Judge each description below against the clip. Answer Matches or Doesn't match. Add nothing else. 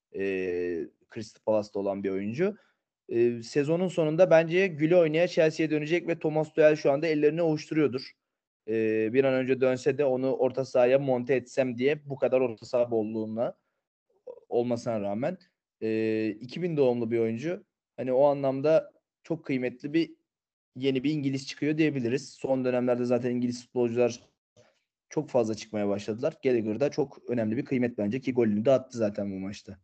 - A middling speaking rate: Doesn't match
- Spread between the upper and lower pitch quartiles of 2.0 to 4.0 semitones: Doesn't match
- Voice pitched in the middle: Doesn't match